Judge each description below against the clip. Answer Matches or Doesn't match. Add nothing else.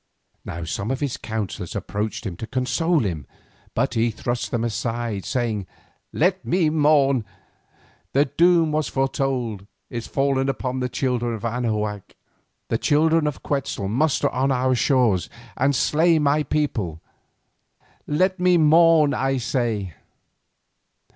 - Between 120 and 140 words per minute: Matches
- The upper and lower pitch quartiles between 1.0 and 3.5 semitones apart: Doesn't match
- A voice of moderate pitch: Doesn't match